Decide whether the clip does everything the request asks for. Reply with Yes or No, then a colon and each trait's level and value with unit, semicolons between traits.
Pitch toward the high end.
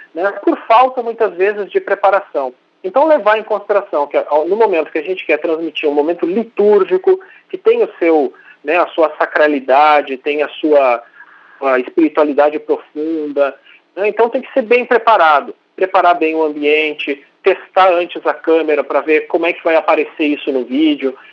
No: medium, 175 Hz